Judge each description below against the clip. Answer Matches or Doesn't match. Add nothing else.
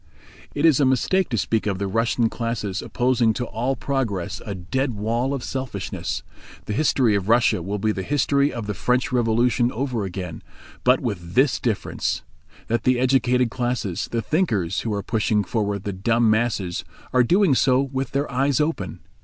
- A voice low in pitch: Matches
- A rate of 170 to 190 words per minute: Matches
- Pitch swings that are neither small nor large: Matches